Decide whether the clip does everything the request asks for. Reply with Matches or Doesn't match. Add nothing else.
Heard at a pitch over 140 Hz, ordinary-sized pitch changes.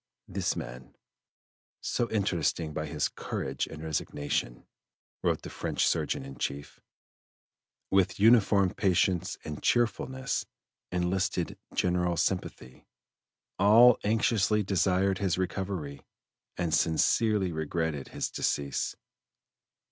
Doesn't match